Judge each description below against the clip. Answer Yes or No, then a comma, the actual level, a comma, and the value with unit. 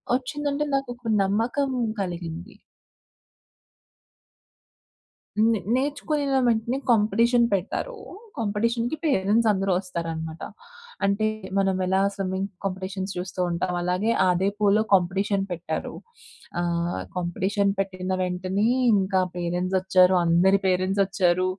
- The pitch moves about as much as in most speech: Yes, average, 3.4 semitones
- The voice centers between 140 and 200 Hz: Yes, high, 195 Hz